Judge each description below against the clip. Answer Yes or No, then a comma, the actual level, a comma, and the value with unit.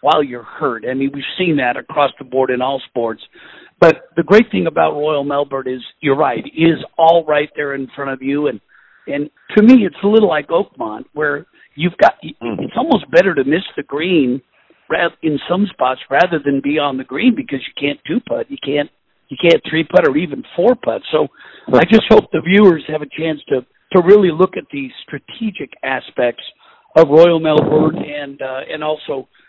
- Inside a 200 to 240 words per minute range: Yes, fast, 205 wpm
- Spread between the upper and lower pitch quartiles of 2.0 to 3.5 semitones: No, average, 4.2 semitones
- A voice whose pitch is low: No, medium, 150 Hz